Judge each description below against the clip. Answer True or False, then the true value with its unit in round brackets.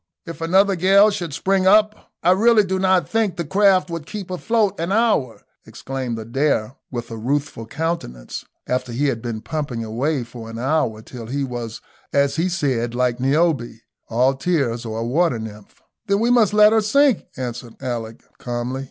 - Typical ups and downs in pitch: False (7.9 semitones)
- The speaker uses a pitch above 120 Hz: True (140 Hz)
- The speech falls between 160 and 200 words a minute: True (180 wpm)